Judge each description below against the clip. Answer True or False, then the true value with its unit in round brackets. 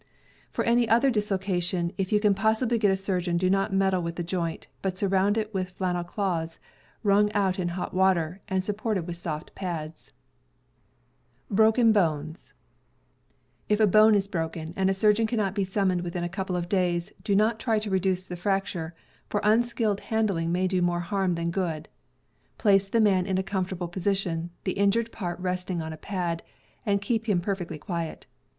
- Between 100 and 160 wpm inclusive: False (180 wpm)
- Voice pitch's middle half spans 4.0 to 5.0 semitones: False (2.9 semitones)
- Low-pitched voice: False (190 Hz)